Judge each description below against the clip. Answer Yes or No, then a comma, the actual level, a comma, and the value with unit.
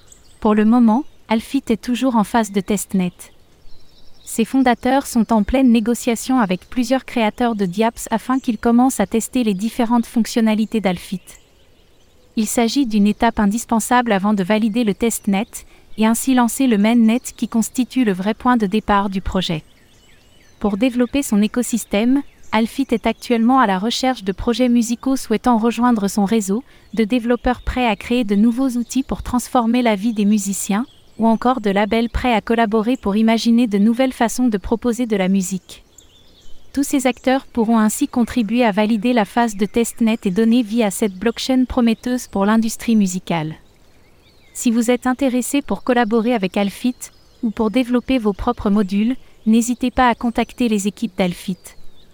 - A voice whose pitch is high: Yes, high, 230 Hz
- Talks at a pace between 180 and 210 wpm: No, average, 165 wpm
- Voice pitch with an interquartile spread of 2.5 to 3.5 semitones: Yes, average, 2.9 semitones